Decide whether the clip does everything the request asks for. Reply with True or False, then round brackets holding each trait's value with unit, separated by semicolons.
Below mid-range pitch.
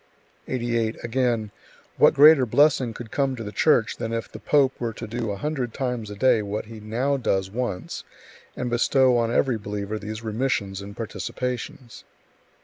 True (115 Hz)